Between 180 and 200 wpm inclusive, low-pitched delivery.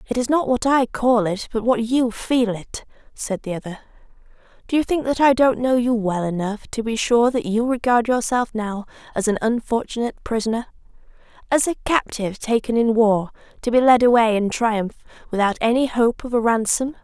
No: average, 190 wpm; high, 235 Hz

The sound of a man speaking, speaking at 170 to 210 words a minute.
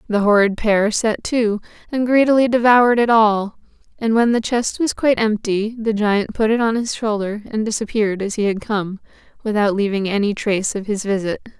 No: female; average, 190 wpm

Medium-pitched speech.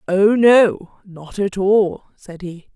No: high, 195 Hz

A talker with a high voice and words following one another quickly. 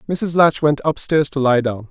No: medium, 145 Hz; fast, 220 wpm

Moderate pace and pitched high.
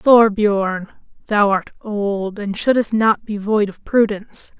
Yes: average, 145 wpm; high, 210 Hz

